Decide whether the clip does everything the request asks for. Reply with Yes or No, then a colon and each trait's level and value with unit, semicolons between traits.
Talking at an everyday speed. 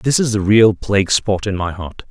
No: fast, 255 wpm